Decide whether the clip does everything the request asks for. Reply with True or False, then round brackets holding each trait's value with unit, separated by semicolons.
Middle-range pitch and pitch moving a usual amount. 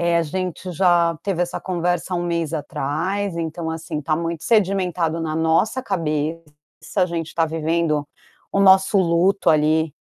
False (170 Hz; 2.2 semitones)